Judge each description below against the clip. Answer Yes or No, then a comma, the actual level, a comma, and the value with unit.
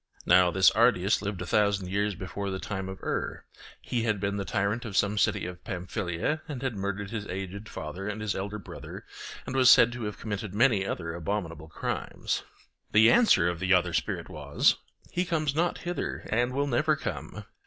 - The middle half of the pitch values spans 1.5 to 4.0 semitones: Yes, average, 3.6 semitones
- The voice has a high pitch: No, low, 100 Hz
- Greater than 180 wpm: Yes, average, 195 wpm